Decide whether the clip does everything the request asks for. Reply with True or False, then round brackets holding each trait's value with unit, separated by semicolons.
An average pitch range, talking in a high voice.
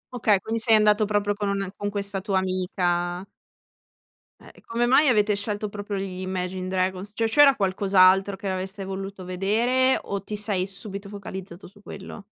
False (1.9 semitones; 200 Hz)